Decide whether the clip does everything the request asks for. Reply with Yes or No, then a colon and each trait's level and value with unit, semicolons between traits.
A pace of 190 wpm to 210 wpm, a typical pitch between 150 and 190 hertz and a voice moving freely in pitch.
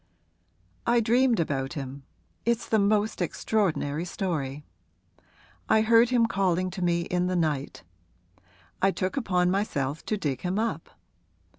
No: slow, 135 wpm; medium, 185 Hz; wide, 5.8 semitones